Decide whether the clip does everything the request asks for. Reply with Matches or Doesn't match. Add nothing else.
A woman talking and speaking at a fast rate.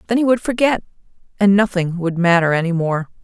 Doesn't match